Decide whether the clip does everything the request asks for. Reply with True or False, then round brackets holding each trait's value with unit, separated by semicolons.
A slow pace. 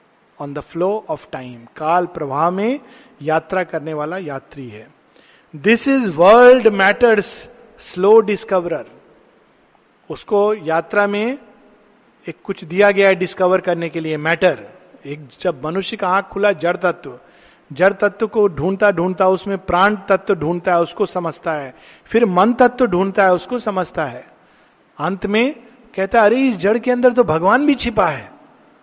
False (155 wpm)